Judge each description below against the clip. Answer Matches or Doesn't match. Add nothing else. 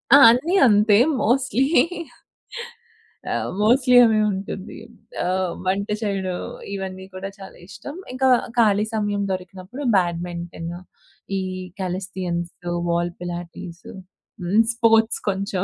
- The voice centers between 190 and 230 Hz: Matches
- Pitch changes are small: Doesn't match